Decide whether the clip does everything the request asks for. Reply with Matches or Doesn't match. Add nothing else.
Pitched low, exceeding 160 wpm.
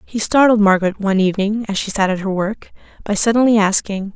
Doesn't match